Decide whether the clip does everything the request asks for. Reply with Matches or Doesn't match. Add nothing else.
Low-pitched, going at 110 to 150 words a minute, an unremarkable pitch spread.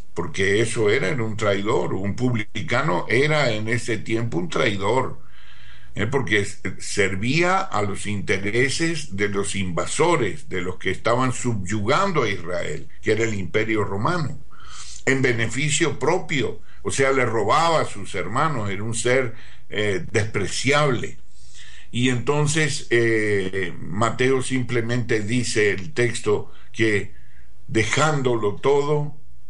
Matches